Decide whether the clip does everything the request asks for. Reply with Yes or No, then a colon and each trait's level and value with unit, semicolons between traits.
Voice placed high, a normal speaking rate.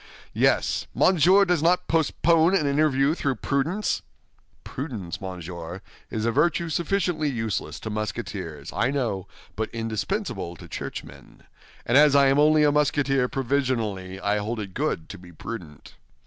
No: low, 135 Hz; average, 145 wpm